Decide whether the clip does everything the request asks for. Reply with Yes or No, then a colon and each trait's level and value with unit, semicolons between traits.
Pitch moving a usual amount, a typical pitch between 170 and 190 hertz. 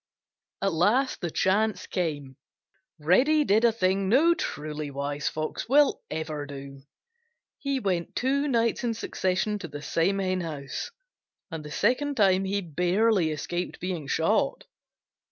No: wide, 6.1 semitones; medium, 185 Hz